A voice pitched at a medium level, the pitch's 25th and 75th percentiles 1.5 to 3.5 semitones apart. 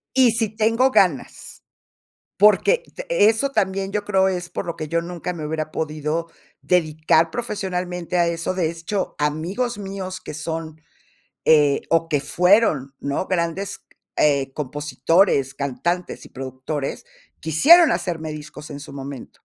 No: medium, 170 Hz; average, 4.3 semitones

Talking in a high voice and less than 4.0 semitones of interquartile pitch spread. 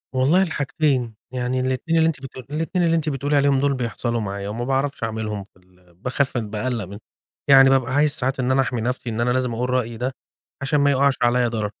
No: low, 130 Hz; average, 3.2 semitones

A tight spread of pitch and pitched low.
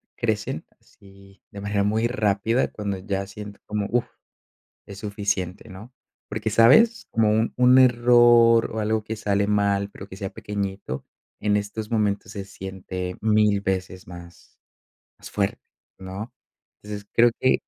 Yes: narrow, 2.2 semitones; low, 105 Hz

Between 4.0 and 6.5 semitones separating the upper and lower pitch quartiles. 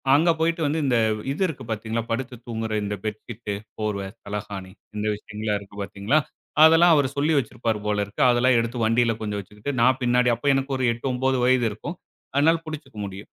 Yes: average, 4.5 semitones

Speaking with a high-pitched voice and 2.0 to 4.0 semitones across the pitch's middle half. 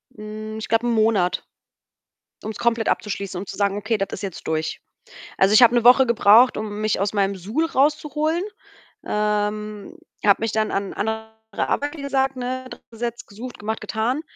Yes: high, 220 Hz; average, 2.9 semitones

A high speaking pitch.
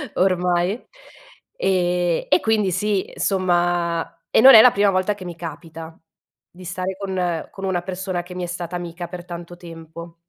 No: medium, 180 Hz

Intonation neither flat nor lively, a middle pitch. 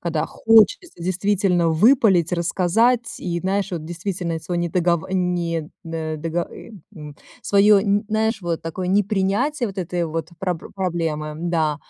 Yes: average, 3.3 semitones; medium, 175 Hz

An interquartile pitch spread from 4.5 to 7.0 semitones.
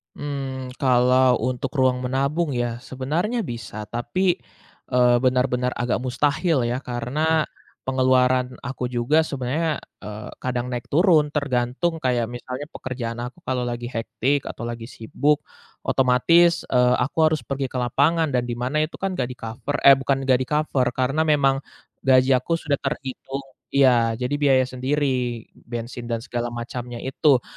No: average, 2.7 semitones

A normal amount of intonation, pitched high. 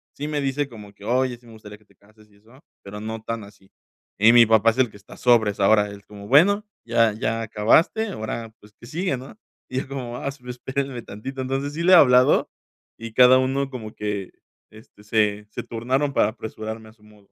No: average, 3.7 semitones; low, 115 Hz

